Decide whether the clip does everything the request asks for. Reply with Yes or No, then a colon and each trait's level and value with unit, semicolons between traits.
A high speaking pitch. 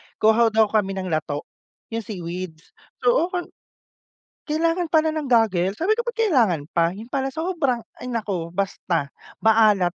Yes: high, 220 Hz